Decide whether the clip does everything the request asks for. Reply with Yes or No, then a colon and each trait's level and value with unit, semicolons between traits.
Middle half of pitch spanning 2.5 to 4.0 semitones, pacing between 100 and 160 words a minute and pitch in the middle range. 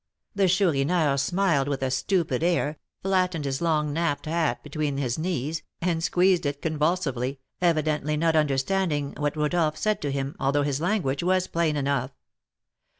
Yes: average, 3.6 semitones; average, 150 wpm; medium, 155 Hz